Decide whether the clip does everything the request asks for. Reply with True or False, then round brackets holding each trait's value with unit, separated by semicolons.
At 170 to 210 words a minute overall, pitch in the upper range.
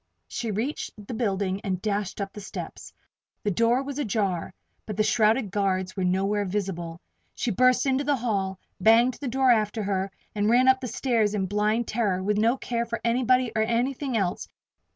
True (185 wpm; 215 Hz)